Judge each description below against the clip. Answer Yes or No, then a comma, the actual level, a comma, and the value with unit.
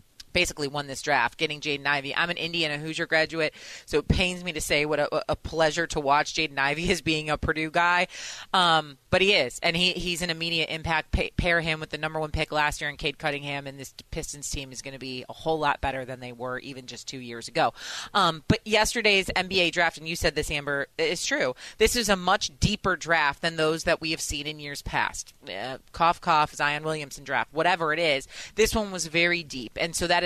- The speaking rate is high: Yes, fast, 235 wpm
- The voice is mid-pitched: Yes, medium, 155 Hz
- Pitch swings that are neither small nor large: Yes, average, 3.1 semitones